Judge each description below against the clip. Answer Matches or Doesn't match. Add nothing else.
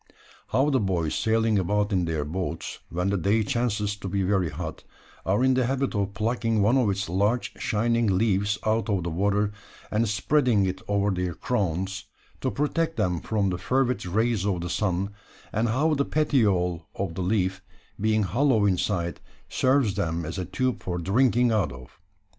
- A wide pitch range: Doesn't match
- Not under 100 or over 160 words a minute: Doesn't match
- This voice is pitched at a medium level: Doesn't match